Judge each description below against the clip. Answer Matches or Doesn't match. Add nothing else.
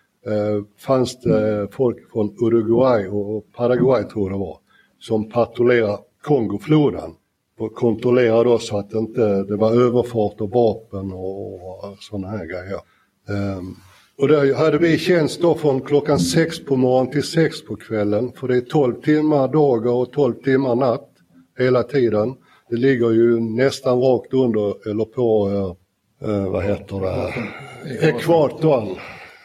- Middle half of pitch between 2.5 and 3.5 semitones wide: Doesn't match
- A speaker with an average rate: Matches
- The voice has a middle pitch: Doesn't match